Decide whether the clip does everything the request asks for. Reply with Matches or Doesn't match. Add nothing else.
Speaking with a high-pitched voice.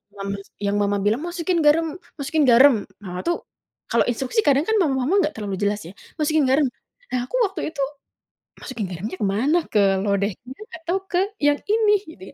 Matches